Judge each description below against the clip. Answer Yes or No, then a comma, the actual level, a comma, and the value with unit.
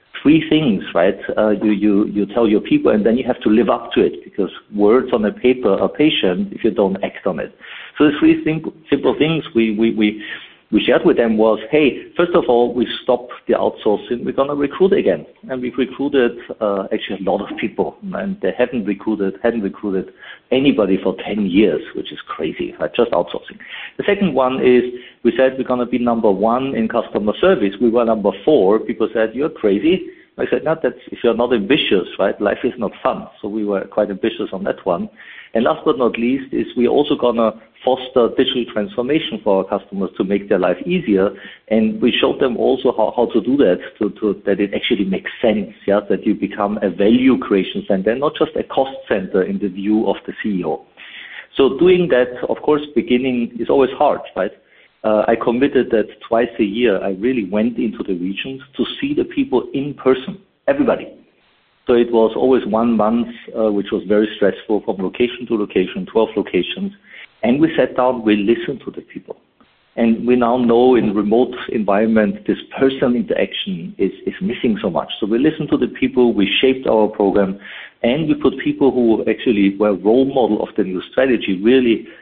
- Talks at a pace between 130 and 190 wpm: No, average, 200 wpm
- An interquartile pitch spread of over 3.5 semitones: Yes, average, 4.1 semitones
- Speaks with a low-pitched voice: Yes, low, 120 Hz